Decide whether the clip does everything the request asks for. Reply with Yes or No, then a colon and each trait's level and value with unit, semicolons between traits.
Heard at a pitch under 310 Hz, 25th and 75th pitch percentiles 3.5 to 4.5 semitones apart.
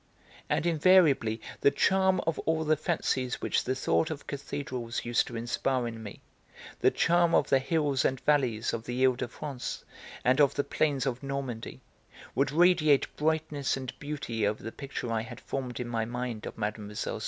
Yes: low, 135 Hz; average, 4.1 semitones